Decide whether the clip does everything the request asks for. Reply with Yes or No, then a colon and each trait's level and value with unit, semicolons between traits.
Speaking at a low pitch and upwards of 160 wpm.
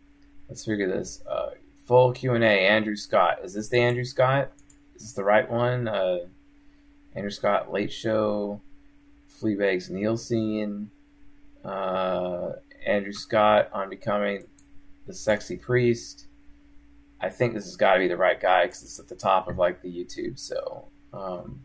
No: low, 105 Hz; average, 150 wpm